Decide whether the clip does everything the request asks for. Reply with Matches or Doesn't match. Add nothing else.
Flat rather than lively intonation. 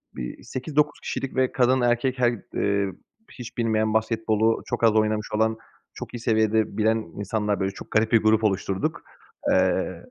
Matches